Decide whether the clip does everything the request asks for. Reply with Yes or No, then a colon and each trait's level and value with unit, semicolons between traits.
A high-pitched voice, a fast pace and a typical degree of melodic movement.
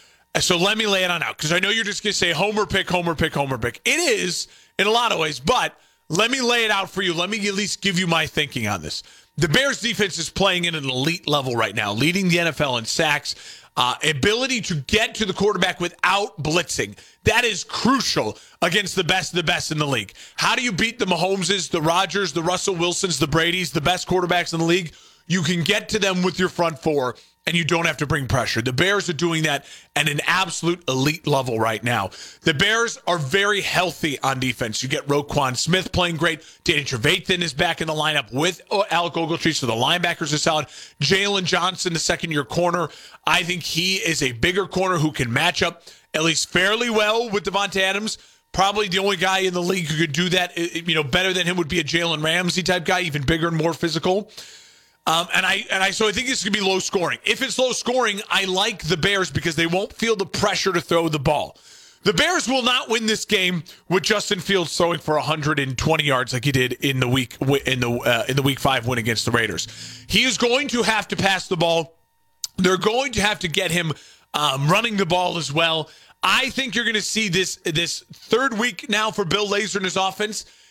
No: medium, 175 Hz; fast, 230 wpm; average, 4.0 semitones